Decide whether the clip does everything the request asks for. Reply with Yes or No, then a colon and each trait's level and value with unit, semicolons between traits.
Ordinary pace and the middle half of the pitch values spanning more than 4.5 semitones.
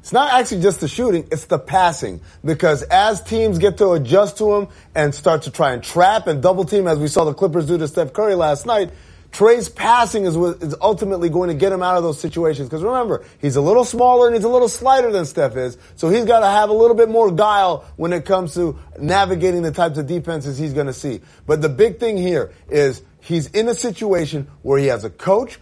No: fast, 240 wpm; wide, 5.4 semitones